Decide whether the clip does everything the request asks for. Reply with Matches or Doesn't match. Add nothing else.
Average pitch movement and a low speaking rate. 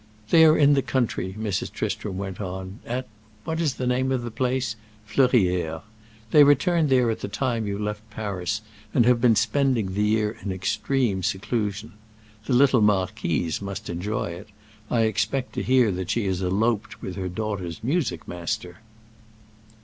Doesn't match